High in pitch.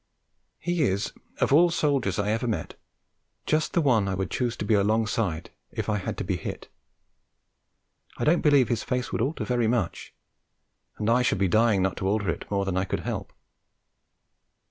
No: low, 110 Hz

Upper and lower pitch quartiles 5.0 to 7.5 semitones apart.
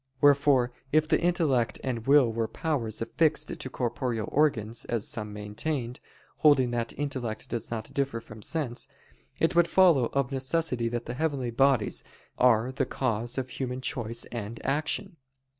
No: average, 3.8 semitones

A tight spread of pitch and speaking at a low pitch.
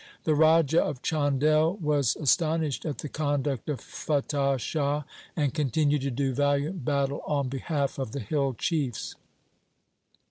No: narrow, 2.0 semitones; medium, 145 Hz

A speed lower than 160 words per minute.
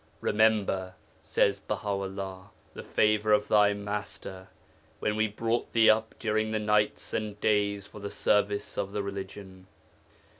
Yes: average, 145 wpm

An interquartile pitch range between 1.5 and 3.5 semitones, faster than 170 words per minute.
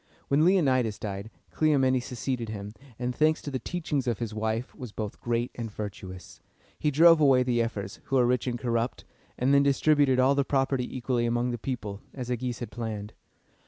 Yes: average, 3.0 semitones; average, 190 wpm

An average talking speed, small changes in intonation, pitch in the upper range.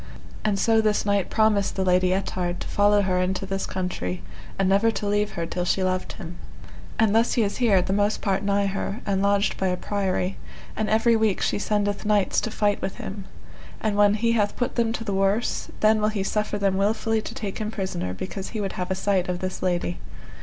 No: fast, 225 wpm; narrow, 2.1 semitones; high, 200 Hz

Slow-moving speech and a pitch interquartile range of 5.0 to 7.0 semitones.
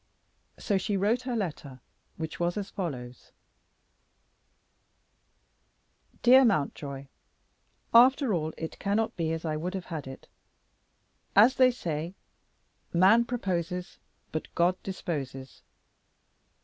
Yes: slow, 110 wpm; average, 5.3 semitones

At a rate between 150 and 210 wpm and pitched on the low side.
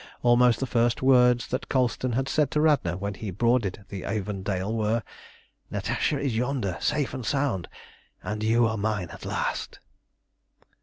Yes: average, 155 wpm; low, 115 Hz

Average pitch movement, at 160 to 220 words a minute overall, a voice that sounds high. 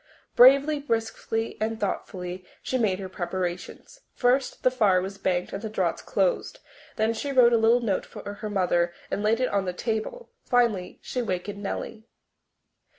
Yes: average, 4.4 semitones; average, 165 wpm; high, 215 Hz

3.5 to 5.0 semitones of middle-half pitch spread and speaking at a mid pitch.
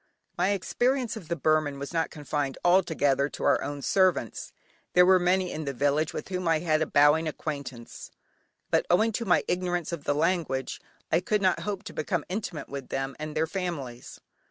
Yes: average, 4.1 semitones; medium, 160 Hz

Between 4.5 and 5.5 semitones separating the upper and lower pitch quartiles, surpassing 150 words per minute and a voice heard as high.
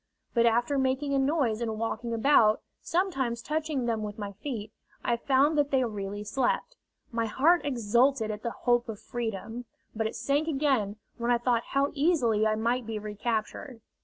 No: average, 3.9 semitones; average, 175 wpm; high, 240 Hz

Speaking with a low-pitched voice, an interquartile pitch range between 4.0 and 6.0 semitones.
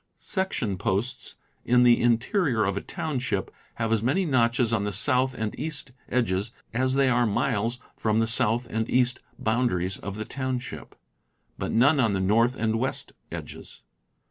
No: low, 120 Hz; average, 2.9 semitones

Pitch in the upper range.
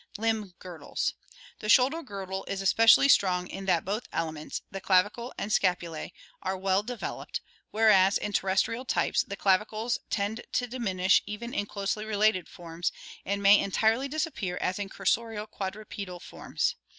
Yes: high, 200 Hz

